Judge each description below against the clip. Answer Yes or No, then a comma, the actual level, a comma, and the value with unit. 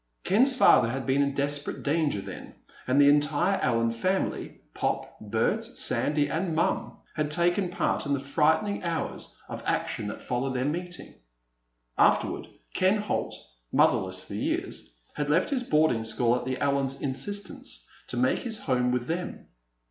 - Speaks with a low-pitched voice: No, medium, 145 Hz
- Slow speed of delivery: No, average, 150 wpm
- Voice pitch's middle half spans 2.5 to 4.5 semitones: No, average, 5.3 semitones